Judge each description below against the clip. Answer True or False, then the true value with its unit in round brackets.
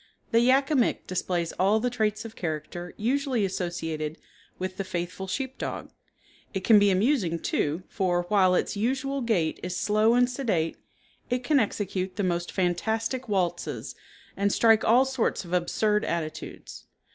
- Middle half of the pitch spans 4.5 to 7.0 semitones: True (5.0 semitones)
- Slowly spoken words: False (160 wpm)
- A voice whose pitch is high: True (200 Hz)